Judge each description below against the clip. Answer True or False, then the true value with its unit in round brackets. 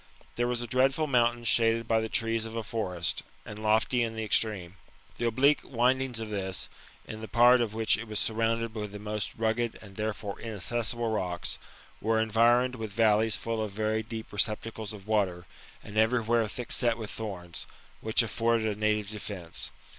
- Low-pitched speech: True (110 Hz)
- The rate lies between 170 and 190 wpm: True (180 wpm)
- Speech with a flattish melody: True (1.6 semitones)